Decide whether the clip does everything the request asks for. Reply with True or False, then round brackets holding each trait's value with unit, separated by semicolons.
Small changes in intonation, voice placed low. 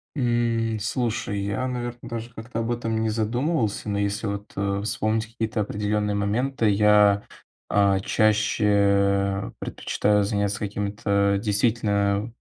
True (2.0 semitones; 105 Hz)